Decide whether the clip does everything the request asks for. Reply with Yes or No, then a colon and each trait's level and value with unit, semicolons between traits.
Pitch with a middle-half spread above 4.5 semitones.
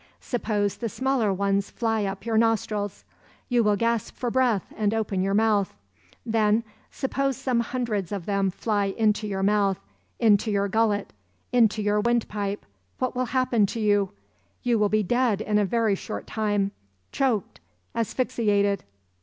No: narrow, 2.5 semitones